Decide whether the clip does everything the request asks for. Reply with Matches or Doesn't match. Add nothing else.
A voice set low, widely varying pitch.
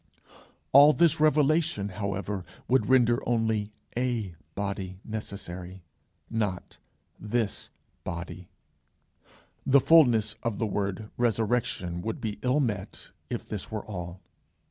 Doesn't match